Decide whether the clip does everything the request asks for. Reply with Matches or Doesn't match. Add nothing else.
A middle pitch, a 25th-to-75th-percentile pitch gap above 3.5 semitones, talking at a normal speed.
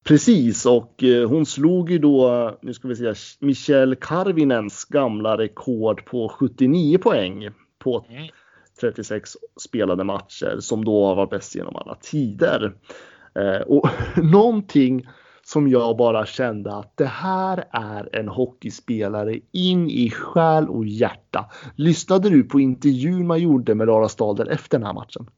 Doesn't match